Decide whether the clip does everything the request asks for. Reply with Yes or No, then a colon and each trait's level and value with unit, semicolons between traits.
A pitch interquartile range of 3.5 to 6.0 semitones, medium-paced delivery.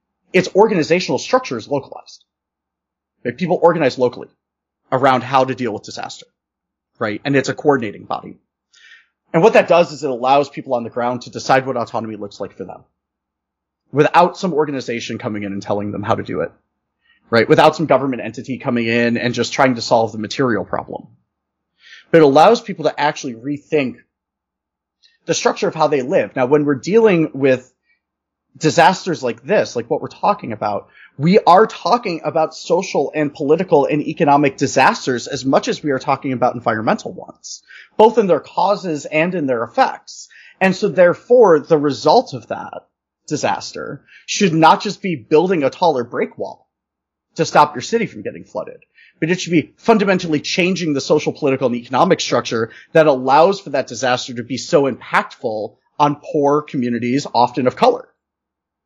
Yes: average, 5.3 semitones; average, 175 wpm